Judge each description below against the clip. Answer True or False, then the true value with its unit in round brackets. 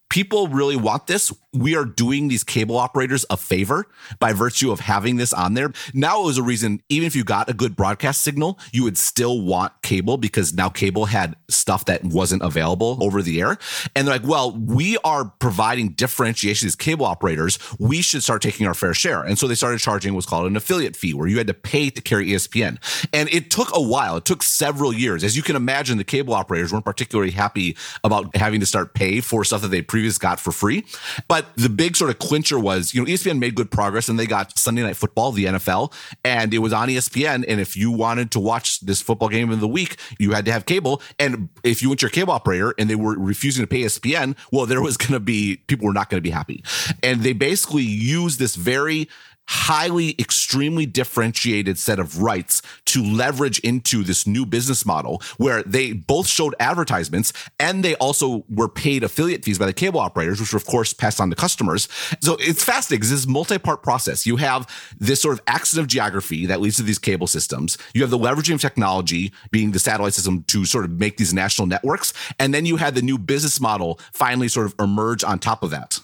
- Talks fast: True (225 wpm)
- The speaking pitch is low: True (115 Hz)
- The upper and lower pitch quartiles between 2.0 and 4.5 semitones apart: False (4.9 semitones)